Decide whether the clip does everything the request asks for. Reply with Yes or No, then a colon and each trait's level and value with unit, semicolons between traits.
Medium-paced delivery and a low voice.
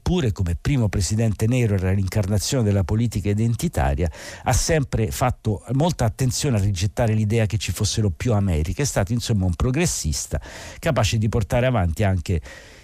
Yes: average, 155 wpm; low, 110 Hz